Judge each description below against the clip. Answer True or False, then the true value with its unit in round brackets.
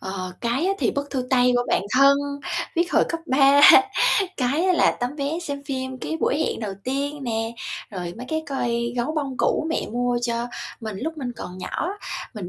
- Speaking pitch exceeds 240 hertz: True (260 Hz)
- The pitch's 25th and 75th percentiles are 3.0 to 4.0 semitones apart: True (3.4 semitones)